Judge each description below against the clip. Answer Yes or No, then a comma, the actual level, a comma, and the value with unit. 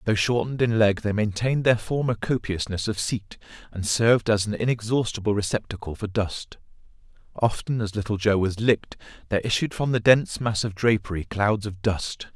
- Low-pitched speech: Yes, low, 105 Hz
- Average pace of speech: Yes, average, 175 wpm